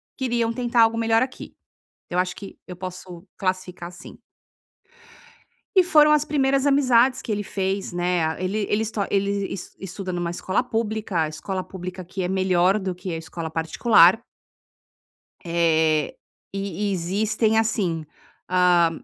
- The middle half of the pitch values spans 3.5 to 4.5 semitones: Yes, average, 4.1 semitones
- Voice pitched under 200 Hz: Yes, high, 190 Hz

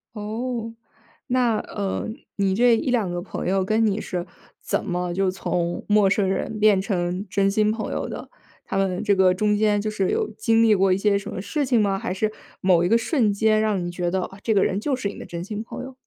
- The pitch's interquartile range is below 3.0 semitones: Yes, narrow, 2.6 semitones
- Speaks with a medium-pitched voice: No, high, 205 Hz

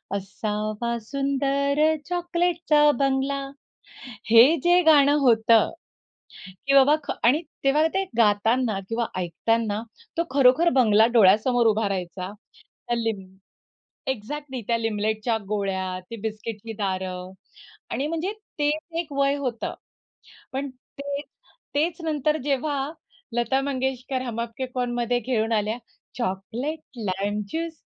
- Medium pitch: No, high, 245 Hz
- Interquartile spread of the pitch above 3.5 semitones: Yes, average, 4.7 semitones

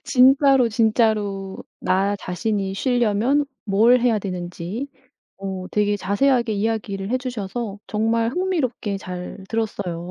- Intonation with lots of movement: No, average, 3.8 semitones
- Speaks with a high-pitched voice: Yes, high, 215 Hz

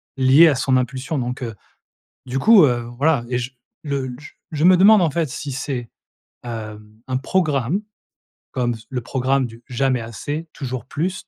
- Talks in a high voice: No, low, 130 Hz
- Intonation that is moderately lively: Yes, average, 3.7 semitones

